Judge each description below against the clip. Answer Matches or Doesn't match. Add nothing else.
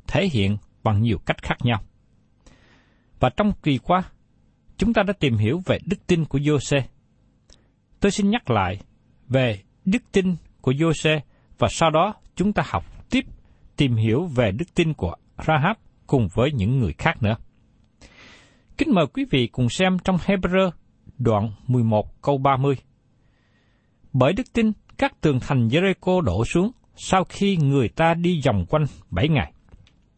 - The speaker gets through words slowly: Matches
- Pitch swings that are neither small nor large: Doesn't match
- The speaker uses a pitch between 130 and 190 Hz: Matches